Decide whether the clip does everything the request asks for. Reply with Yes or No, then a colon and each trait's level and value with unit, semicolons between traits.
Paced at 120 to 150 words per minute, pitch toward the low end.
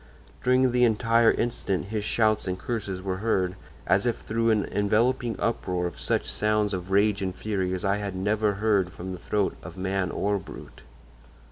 No: average, 180 wpm; low, 105 Hz